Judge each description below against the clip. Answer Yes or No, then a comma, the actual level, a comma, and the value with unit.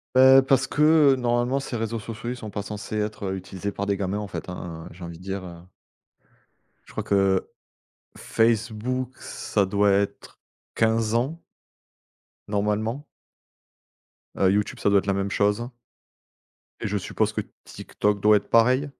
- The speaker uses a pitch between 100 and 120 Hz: Yes, low, 105 Hz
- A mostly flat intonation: No, average, 3.0 semitones